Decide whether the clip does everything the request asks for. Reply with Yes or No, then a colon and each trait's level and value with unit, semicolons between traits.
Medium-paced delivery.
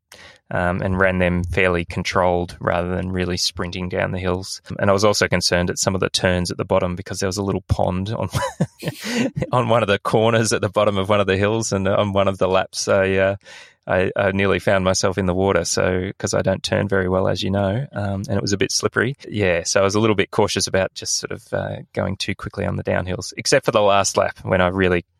No: fast, 250 wpm